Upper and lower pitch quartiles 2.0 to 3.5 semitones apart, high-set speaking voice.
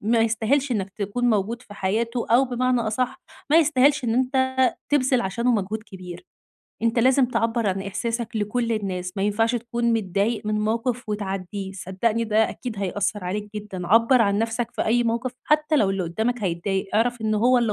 Yes: average, 3.2 semitones; high, 225 Hz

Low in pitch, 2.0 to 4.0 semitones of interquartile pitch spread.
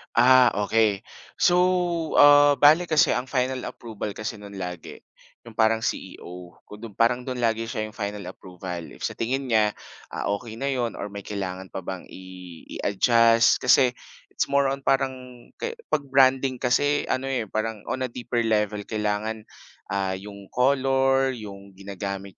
No: low, 115 Hz; average, 4.4 semitones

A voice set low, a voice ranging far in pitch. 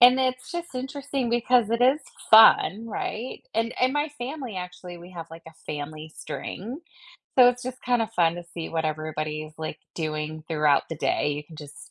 No: medium, 185 Hz; wide, 8.1 semitones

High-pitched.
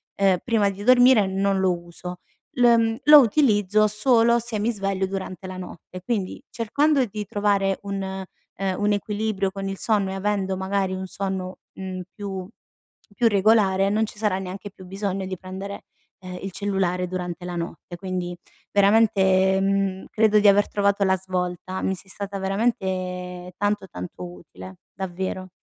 Yes: high, 195 Hz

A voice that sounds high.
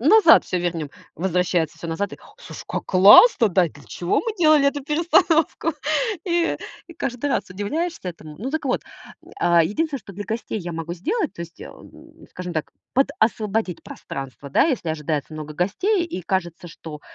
Yes: high, 195 Hz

